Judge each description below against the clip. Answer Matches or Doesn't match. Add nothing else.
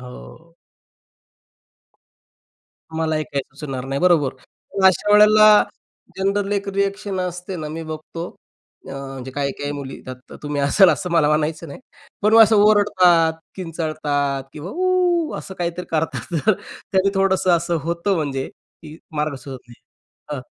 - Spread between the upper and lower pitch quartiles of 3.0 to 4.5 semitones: Doesn't match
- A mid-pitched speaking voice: Matches